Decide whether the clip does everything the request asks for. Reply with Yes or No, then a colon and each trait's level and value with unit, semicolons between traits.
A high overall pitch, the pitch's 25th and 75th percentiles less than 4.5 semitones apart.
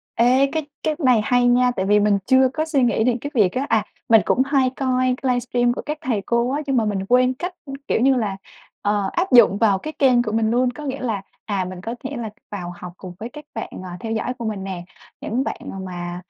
Yes: high, 240 Hz; average, 4.1 semitones